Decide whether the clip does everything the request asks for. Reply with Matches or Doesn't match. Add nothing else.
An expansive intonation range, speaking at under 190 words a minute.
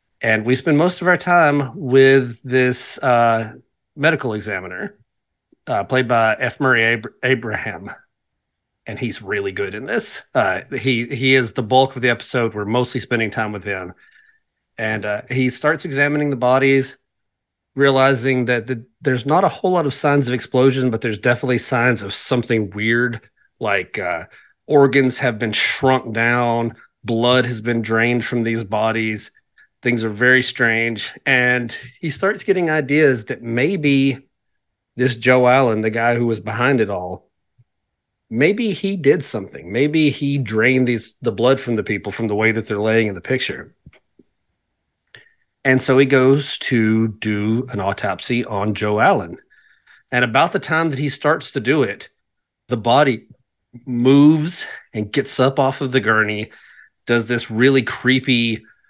Doesn't match